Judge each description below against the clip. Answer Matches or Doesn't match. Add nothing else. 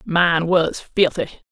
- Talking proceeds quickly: Doesn't match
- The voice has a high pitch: Doesn't match